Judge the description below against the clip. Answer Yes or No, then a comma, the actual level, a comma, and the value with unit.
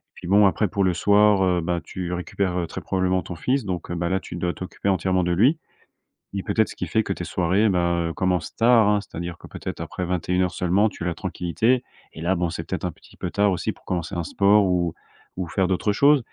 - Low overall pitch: Yes, very low, 95 Hz